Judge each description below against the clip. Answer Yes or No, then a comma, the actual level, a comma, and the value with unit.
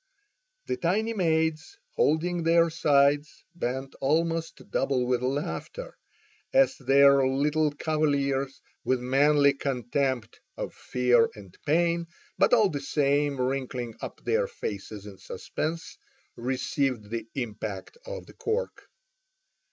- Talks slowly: Yes, slow, 115 wpm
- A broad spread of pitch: No, average, 4.4 semitones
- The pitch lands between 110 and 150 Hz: Yes, medium, 140 Hz